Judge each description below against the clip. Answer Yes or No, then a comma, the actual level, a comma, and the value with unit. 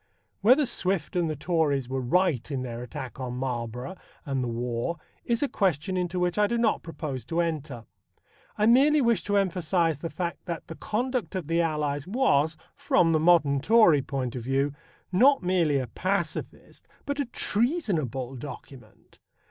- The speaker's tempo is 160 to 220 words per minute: Yes, average, 170 wpm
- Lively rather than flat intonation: Yes, wide, 6.7 semitones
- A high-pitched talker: No, medium, 165 Hz